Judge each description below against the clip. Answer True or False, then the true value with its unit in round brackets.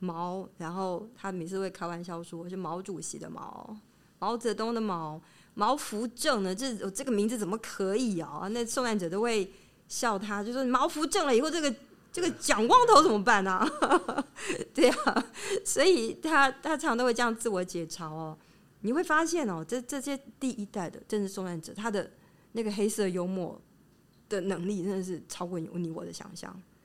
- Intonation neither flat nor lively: False (5.9 semitones)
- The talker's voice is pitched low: False (210 Hz)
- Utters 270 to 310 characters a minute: True (275 characters per minute)